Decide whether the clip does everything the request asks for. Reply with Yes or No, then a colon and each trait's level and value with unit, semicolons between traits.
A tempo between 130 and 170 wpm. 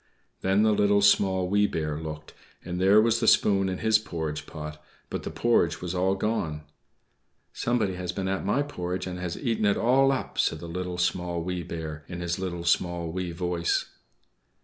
No: average, 190 wpm